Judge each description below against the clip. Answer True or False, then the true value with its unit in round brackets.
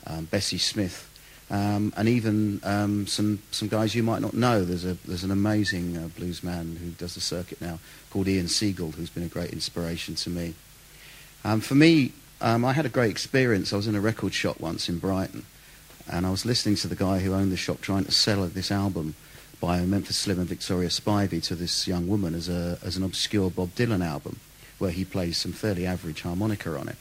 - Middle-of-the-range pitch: False (95 Hz)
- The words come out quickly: True (220 wpm)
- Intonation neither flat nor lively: True (3.3 semitones)